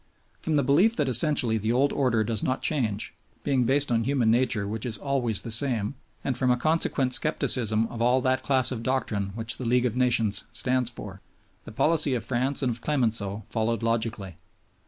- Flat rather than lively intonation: No, average, 3.1 semitones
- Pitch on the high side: No, low, 120 Hz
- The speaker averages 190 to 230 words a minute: Yes, average, 195 wpm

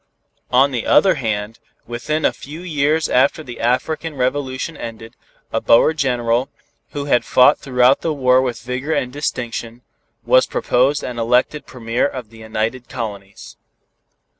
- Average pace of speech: Yes, average, 145 wpm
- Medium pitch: No, low, 125 Hz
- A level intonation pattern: No, average, 3.4 semitones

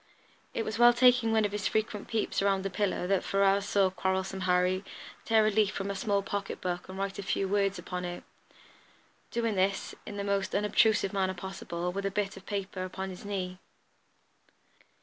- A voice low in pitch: No, high, 195 Hz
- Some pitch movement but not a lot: No, narrow, 1.6 semitones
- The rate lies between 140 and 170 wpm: No, average, 190 wpm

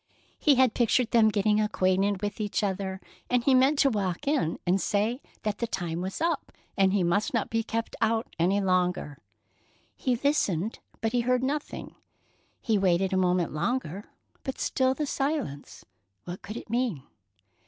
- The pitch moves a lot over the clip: No, average, 5.0 semitones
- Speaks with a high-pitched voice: Yes, high, 210 Hz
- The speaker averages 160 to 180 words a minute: Yes, average, 170 wpm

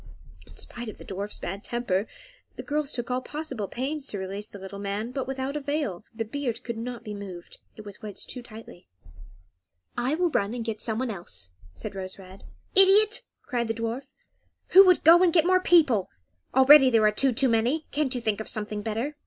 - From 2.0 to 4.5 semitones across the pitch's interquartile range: No, average, 5.2 semitones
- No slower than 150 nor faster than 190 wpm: No, average, 200 wpm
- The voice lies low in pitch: No, high, 235 Hz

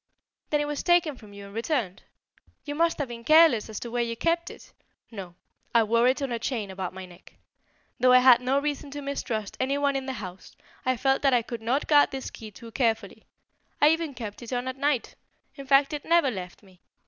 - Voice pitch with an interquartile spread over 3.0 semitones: Yes, average, 4.3 semitones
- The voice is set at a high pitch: Yes, very high, 255 Hz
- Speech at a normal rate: No, fast, 230 wpm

